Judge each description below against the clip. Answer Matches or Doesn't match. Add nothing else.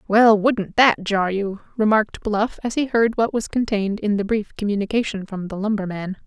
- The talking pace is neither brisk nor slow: Matches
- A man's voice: Doesn't match